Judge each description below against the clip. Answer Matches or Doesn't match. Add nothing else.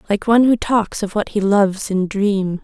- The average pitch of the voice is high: Matches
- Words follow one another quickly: Matches